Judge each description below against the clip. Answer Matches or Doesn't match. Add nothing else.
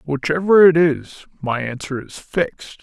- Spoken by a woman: Doesn't match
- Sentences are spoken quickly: Doesn't match